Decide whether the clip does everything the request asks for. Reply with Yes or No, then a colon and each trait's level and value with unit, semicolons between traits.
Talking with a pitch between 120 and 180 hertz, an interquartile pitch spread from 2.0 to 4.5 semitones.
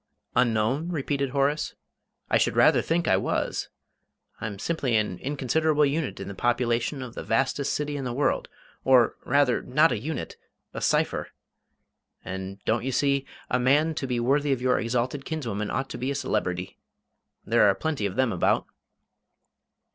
Yes: low, 130 Hz; average, 3.8 semitones